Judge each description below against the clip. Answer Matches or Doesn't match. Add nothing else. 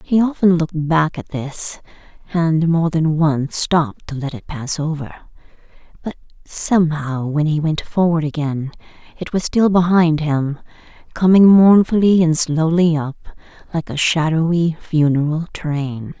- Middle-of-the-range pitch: Matches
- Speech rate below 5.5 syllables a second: Matches